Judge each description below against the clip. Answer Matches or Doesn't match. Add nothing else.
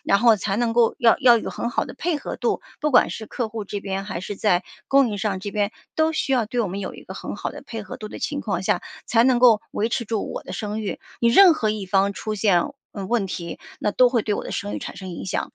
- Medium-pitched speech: Doesn't match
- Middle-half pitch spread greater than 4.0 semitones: Doesn't match